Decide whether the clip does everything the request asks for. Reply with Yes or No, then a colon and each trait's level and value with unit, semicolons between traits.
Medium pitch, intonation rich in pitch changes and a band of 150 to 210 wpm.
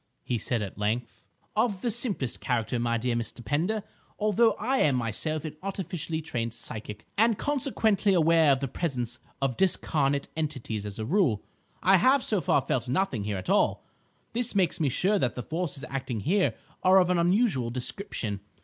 Yes: medium, 150 Hz; wide, 8.2 semitones; average, 175 wpm